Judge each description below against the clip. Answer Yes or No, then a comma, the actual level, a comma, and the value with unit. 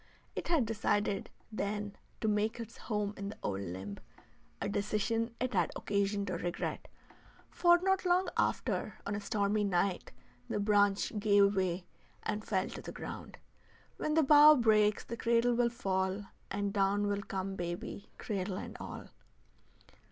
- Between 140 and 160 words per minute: Yes, average, 155 wpm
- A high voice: Yes, high, 205 Hz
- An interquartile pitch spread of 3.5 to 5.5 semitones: No, narrow, 2.5 semitones